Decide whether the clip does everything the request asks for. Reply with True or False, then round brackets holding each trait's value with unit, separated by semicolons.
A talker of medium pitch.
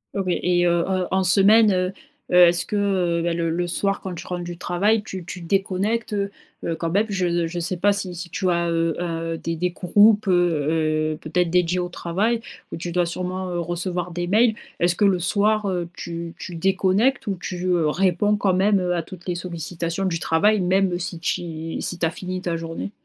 True (180 Hz)